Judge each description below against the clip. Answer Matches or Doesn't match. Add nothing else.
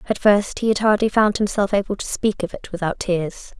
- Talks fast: Matches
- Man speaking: Doesn't match